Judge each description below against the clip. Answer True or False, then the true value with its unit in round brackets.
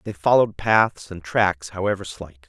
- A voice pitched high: False (95 Hz)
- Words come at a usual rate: True (170 wpm)